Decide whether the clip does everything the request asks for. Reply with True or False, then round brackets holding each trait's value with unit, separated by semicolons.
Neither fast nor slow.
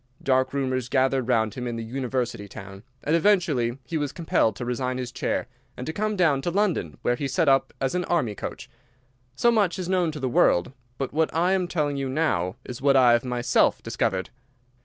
False (210 wpm)